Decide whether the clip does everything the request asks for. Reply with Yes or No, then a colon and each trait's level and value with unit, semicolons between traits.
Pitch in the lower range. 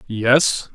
Yes: low, 125 Hz